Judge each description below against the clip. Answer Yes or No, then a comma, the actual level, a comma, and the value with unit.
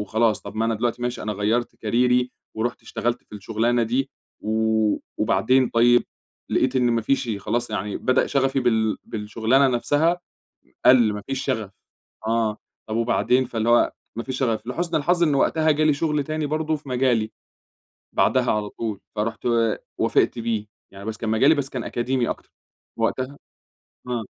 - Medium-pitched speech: No, low, 120 Hz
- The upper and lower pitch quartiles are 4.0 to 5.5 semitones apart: No, average, 3.2 semitones